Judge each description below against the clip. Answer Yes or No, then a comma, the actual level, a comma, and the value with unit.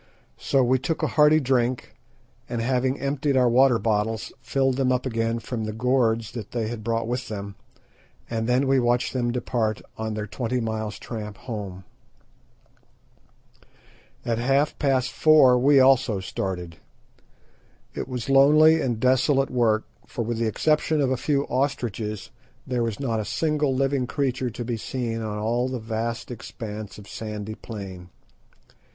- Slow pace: No, average, 155 wpm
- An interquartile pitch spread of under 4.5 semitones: Yes, average, 3.0 semitones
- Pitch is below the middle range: Yes, low, 120 Hz